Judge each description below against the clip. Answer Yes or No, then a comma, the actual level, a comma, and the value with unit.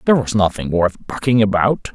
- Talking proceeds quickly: No, average, 185 wpm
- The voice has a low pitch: Yes, low, 105 Hz